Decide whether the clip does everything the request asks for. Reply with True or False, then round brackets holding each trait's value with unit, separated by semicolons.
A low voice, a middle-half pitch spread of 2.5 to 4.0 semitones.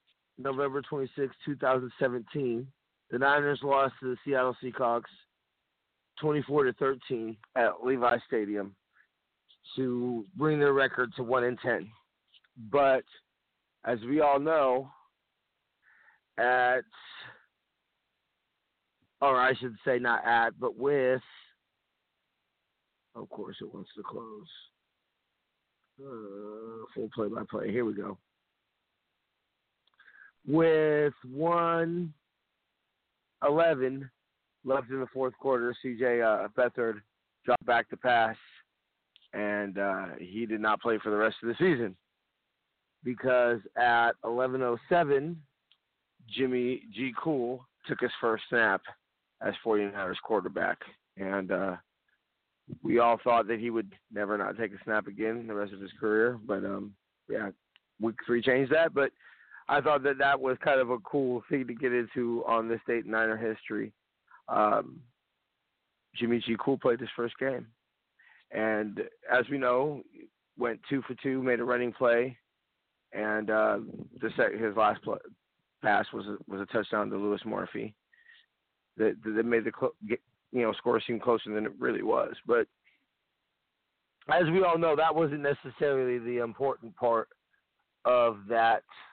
True (125 Hz; 3.3 semitones)